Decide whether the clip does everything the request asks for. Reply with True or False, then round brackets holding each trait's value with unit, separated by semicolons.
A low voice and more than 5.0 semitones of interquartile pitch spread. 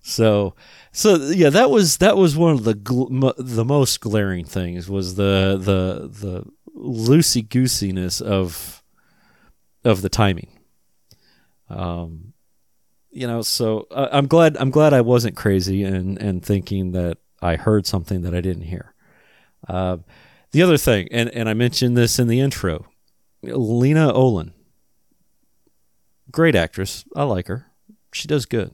True (110 Hz; 5.5 semitones)